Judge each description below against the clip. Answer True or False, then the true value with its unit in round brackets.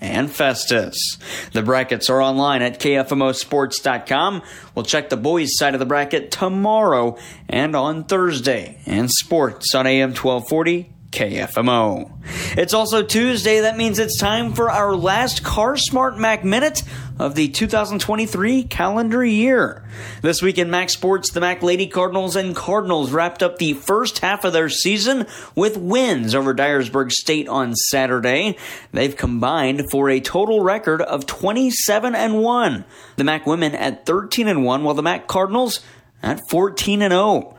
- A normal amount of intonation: False (7.5 semitones)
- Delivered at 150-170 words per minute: True (155 wpm)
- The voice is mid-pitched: True (175 Hz)